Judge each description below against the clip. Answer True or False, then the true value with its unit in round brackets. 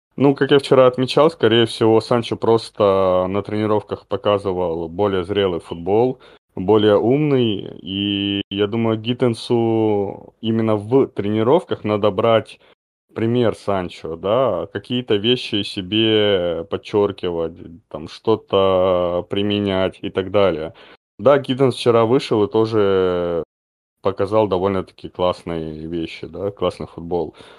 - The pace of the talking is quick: False (115 wpm)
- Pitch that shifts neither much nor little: True (3.0 semitones)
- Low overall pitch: True (105 Hz)